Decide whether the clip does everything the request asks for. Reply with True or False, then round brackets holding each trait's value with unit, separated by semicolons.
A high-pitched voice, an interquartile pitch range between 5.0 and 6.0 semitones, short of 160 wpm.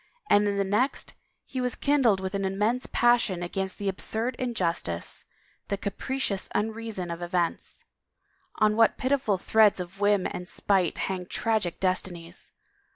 False (200 Hz; 3.6 semitones; 145 wpm)